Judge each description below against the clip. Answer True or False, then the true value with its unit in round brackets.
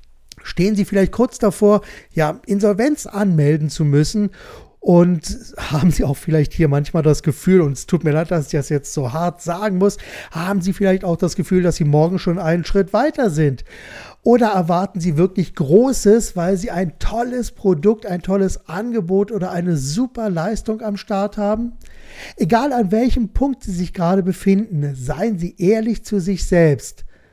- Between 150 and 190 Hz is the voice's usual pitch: True (185 Hz)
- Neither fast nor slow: True (175 wpm)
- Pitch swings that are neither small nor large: True (4.5 semitones)